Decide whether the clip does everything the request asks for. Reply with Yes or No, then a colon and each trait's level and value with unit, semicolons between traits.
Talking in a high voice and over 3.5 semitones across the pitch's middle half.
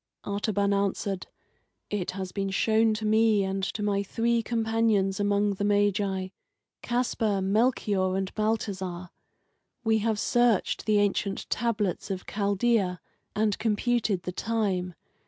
No: high, 205 Hz; narrow, 2.4 semitones